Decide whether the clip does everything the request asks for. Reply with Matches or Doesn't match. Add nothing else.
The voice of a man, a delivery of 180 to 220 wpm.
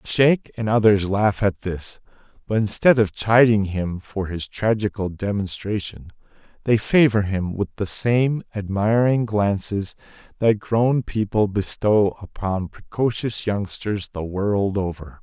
Doesn't match